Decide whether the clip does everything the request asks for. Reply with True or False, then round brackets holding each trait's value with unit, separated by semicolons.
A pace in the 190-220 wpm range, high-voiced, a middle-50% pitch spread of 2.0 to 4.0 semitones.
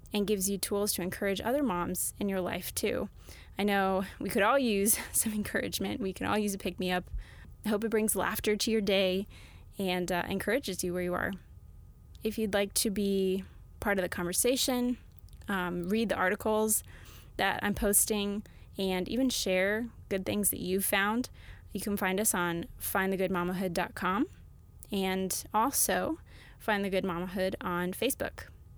False (165 wpm; 195 Hz; 2.7 semitones)